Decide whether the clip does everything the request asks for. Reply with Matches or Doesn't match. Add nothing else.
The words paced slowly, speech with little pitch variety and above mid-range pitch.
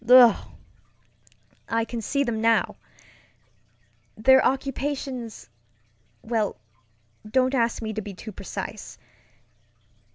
Doesn't match